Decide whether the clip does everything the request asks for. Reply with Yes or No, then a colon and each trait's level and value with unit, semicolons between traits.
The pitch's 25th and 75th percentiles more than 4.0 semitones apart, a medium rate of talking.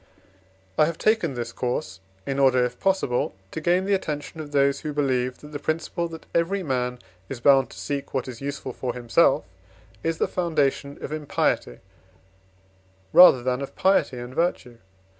Yes: average, 4.6 semitones; average, 170 wpm